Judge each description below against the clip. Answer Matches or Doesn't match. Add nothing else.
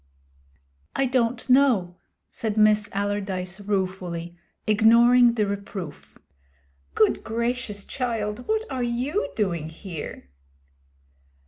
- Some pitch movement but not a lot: Matches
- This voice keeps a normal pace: Doesn't match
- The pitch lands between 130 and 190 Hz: Doesn't match